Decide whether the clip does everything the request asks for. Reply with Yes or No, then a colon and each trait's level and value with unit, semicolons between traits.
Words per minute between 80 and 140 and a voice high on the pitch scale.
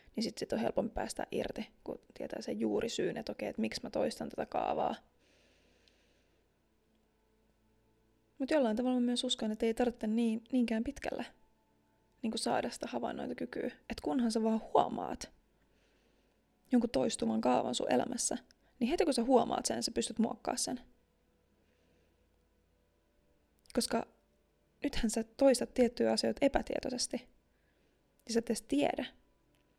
Yes: average, 135 wpm; high, 225 Hz